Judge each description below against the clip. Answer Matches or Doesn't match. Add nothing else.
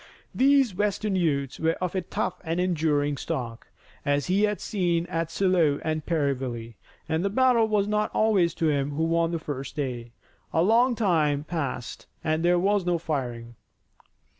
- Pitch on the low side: Doesn't match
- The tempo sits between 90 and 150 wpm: Doesn't match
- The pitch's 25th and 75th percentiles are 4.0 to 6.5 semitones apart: Matches